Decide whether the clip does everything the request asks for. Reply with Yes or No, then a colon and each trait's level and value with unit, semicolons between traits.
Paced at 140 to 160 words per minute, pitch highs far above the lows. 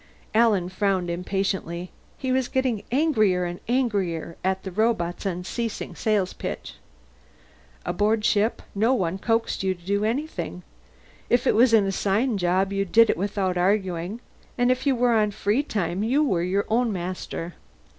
No: average, 155 wpm; average, 4.1 semitones